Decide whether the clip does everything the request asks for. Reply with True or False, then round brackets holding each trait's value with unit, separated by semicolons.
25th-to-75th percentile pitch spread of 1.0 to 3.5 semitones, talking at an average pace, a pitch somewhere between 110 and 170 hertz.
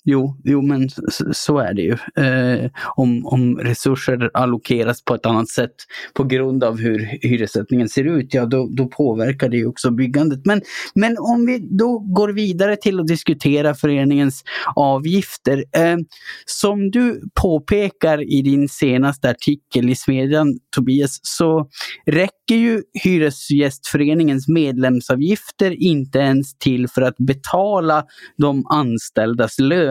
False (4.3 semitones; 135 wpm; 140 Hz)